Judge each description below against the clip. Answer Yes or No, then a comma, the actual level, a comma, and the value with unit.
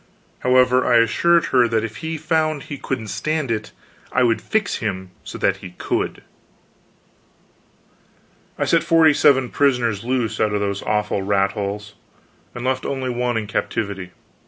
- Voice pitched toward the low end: Yes, low, 120 Hz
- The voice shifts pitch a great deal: No, average, 4.2 semitones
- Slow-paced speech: No, average, 155 wpm